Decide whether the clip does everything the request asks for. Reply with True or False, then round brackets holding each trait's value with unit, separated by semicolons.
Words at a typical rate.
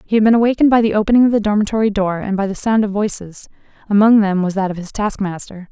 False (240 wpm)